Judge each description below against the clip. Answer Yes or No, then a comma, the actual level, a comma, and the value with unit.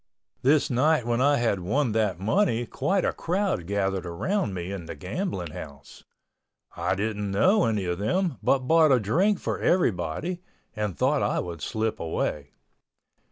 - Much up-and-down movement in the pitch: Yes, wide, 8.7 semitones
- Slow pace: No, average, 160 wpm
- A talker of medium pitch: No, low, 110 Hz